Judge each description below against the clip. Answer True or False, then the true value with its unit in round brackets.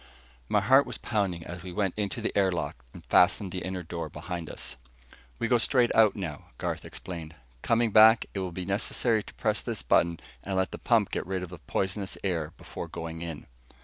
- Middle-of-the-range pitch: False (95 Hz)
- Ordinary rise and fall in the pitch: True (3.6 semitones)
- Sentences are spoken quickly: True (210 wpm)